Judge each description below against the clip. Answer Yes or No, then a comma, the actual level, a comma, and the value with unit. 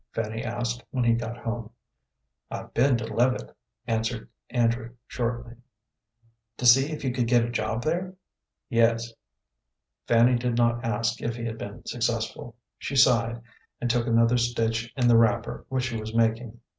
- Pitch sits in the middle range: No, low, 115 Hz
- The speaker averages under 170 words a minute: Yes, average, 160 wpm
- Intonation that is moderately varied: No, narrow, 1.0 semitones